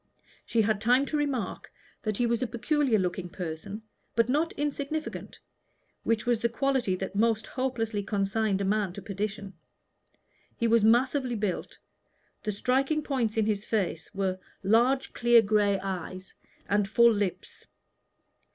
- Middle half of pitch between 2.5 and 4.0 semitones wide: Yes, average, 3.7 semitones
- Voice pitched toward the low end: No, high, 220 Hz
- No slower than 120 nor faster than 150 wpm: Yes, average, 145 wpm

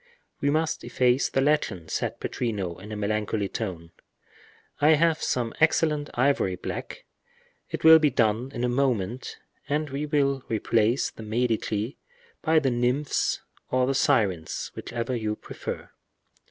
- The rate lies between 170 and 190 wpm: No, average, 140 wpm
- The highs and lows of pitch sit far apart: No, average, 4.9 semitones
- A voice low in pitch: Yes, low, 125 Hz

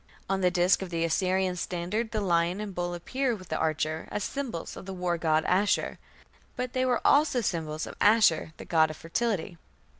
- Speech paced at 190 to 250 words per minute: Yes, fast, 205 wpm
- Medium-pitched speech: Yes, medium, 180 Hz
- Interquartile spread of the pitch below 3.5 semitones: No, average, 4.1 semitones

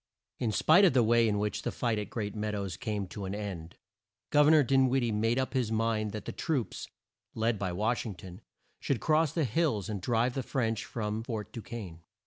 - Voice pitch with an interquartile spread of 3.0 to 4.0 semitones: Yes, average, 3.4 semitones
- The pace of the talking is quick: Yes, fast, 230 wpm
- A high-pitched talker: No, low, 110 Hz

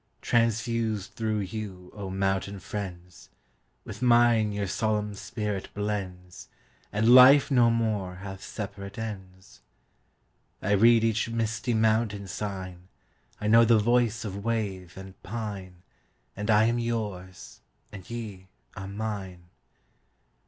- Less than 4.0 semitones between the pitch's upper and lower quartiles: Yes, average, 2.9 semitones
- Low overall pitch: Yes, low, 105 Hz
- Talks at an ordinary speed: No, slow, 105 wpm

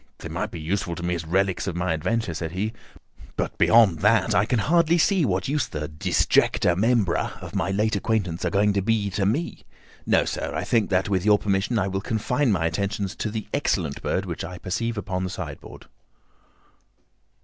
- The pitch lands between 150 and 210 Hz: No, low, 100 Hz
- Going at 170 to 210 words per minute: Yes, average, 200 wpm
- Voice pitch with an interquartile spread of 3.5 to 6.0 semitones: Yes, average, 3.8 semitones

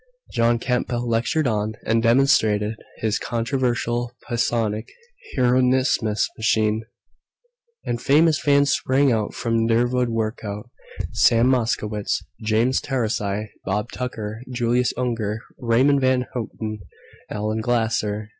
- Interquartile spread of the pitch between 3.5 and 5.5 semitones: No, narrow, 2.5 semitones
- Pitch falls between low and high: No, low, 115 Hz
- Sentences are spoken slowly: Yes, slow, 110 wpm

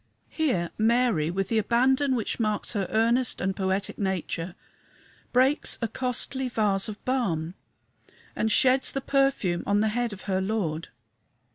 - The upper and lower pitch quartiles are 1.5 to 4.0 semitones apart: No, average, 4.9 semitones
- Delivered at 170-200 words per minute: No, average, 145 wpm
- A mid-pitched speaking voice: No, high, 220 Hz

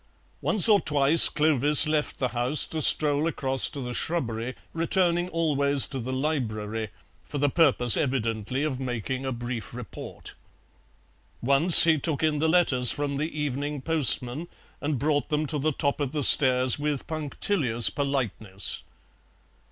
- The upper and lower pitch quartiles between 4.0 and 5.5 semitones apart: No, average, 3.4 semitones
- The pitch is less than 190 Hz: Yes, medium, 140 Hz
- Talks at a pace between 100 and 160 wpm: Yes, average, 150 wpm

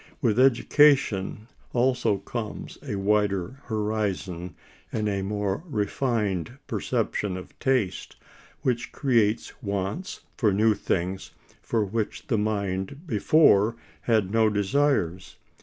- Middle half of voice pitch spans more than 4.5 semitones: No, average, 3.6 semitones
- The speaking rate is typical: No, slow, 110 wpm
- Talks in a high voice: No, low, 105 Hz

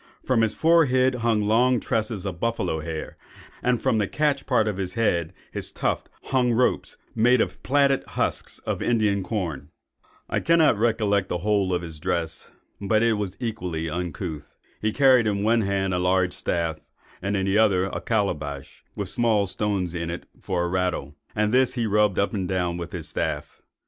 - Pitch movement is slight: No, average, 4.5 semitones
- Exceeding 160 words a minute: Yes, average, 185 wpm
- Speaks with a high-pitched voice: No, low, 100 Hz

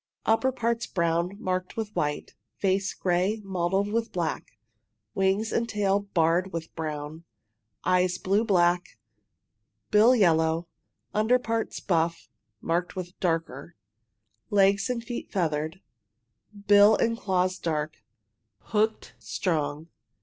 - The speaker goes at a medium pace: No, slow, 115 wpm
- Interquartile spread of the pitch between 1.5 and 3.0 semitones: No, average, 3.9 semitones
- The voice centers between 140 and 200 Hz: Yes, medium, 185 Hz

